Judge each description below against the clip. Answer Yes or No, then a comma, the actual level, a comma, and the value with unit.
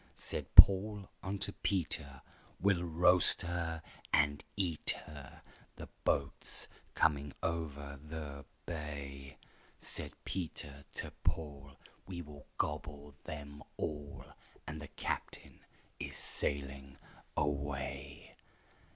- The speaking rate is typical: No, slow, 100 wpm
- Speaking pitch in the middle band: No, very low, 75 Hz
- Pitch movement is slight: No, average, 3.0 semitones